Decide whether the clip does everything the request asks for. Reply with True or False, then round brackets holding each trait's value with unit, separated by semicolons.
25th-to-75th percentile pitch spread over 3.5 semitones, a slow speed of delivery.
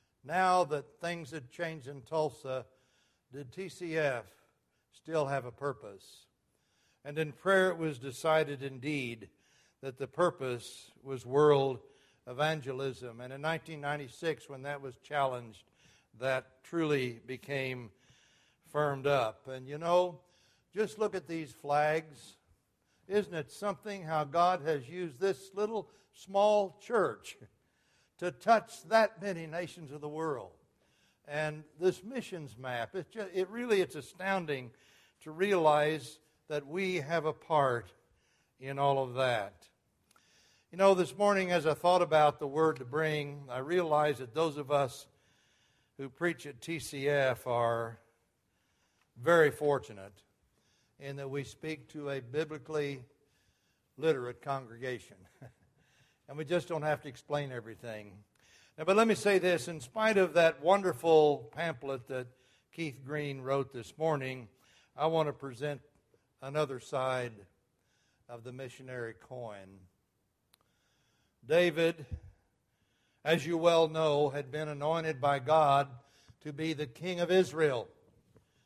True (4.0 semitones; 130 wpm)